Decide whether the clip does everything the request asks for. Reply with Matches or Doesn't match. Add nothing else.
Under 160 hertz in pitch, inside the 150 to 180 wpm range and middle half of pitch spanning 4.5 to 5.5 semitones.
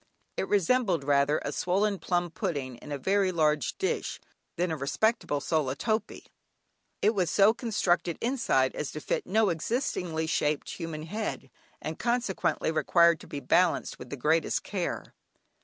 Doesn't match